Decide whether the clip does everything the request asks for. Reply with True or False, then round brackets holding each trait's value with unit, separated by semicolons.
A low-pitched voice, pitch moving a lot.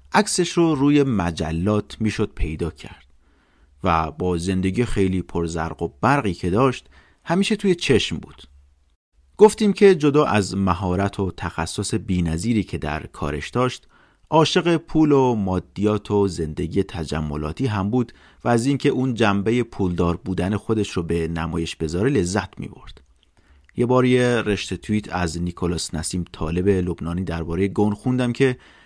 True (95 Hz; 6.9 semitones)